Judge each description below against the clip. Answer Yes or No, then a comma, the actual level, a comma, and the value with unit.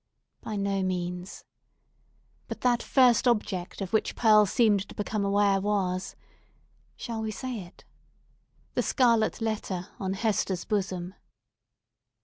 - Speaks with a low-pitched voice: No, high, 205 Hz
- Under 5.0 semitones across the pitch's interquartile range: Yes, average, 2.8 semitones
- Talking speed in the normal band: No, slow, 115 wpm